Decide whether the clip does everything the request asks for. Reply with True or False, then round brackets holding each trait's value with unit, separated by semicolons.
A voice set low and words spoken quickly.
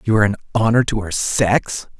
True (110 Hz; 210 wpm)